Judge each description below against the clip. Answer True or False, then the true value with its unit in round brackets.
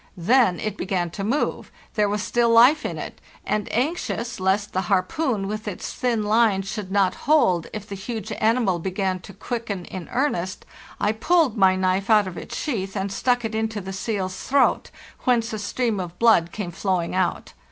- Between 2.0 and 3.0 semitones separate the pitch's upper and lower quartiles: False (3.5 semitones)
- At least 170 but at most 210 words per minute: True (185 wpm)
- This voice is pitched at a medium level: False (205 Hz)